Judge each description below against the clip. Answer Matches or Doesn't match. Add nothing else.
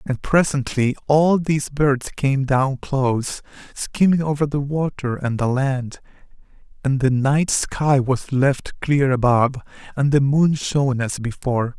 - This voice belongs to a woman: Doesn't match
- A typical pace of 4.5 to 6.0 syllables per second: Doesn't match